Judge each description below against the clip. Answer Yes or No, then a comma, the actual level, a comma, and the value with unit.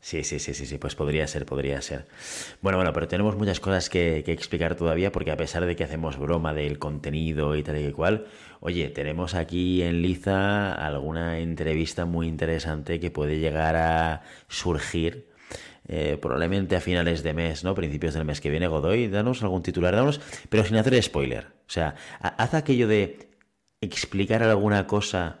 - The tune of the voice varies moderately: Yes, average, 3.8 semitones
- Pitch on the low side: Yes, very low, 85 Hz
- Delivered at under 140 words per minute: No, average, 180 wpm